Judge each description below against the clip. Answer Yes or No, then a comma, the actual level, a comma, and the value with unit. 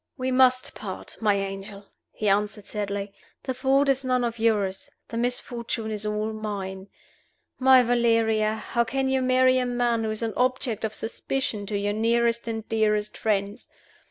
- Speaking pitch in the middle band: No, high, 225 Hz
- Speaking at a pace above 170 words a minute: No, average, 165 wpm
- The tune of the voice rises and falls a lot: No, average, 3.1 semitones